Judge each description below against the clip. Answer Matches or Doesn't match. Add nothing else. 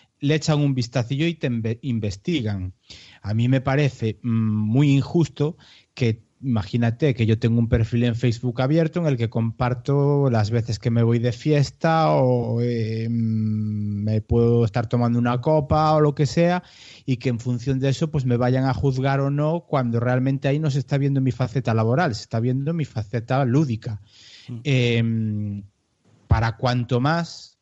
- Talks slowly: Doesn't match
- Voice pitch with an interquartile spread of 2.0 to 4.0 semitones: Matches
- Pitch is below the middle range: Matches